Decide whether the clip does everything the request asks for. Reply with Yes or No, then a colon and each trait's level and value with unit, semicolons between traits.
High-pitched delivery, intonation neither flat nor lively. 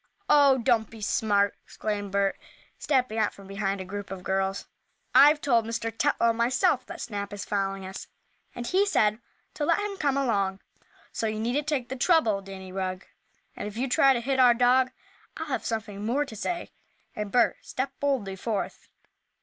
Yes: high, 225 Hz; average, 4.8 semitones